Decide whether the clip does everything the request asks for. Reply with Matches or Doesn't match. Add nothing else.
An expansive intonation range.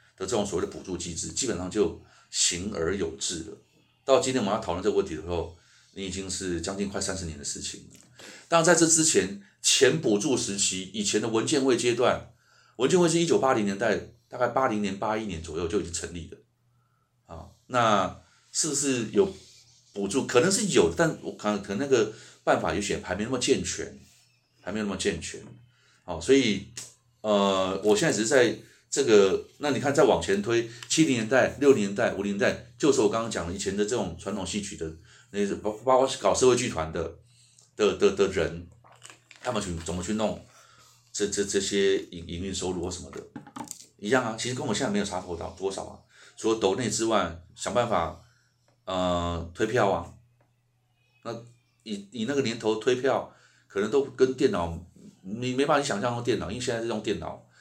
Doesn't match